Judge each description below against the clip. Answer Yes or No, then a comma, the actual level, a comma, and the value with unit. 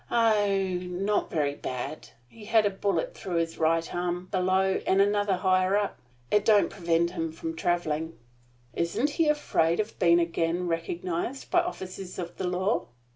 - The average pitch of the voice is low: No, medium, 185 Hz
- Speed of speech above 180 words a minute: No, average, 160 wpm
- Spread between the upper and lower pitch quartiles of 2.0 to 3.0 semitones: No, average, 3.4 semitones